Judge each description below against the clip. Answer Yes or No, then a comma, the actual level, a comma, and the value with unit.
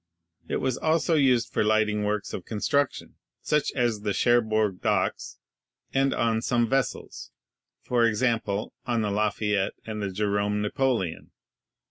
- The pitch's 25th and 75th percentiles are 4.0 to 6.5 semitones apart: No, average, 3.0 semitones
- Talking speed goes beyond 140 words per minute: No, slow, 135 wpm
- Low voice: Yes, low, 110 Hz